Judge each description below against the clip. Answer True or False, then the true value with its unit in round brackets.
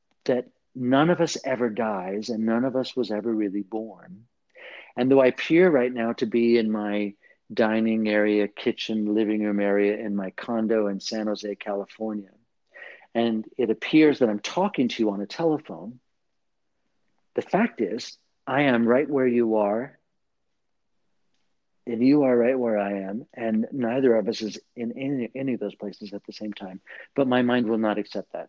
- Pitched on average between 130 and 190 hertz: False (110 Hz)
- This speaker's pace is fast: False (180 wpm)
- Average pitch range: True (3.0 semitones)